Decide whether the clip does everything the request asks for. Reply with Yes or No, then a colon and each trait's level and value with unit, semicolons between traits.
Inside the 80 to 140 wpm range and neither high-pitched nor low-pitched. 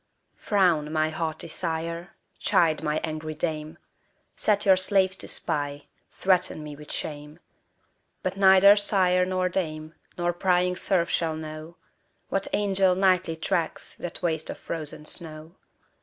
Yes: slow, 135 wpm; medium, 170 Hz